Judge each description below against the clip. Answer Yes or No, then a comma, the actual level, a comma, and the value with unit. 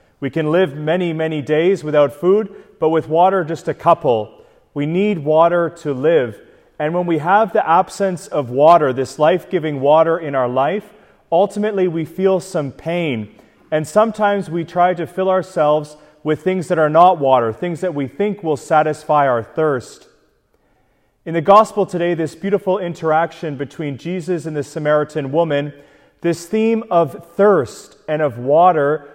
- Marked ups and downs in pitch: No, average, 3.6 semitones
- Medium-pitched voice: Yes, medium, 165 Hz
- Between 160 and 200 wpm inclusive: Yes, average, 165 wpm